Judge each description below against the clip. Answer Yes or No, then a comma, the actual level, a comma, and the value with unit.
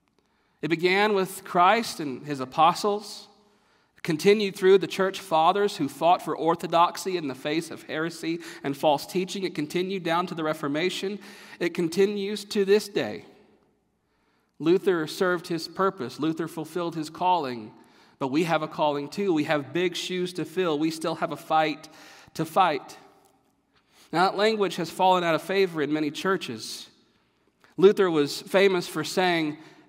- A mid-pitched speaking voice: Yes, medium, 175 Hz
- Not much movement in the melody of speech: No, average, 3.7 semitones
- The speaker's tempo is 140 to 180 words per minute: Yes, average, 155 wpm